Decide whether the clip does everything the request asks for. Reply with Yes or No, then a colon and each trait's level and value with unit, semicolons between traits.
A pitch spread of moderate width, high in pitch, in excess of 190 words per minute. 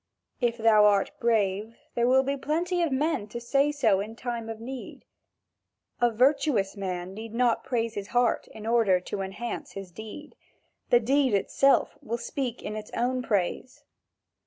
No: average, 3.8 semitones; high, 230 Hz; average, 165 wpm